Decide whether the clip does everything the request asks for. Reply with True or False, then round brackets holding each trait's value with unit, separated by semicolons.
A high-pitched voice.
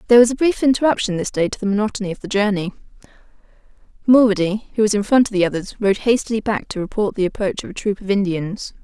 True (205 Hz)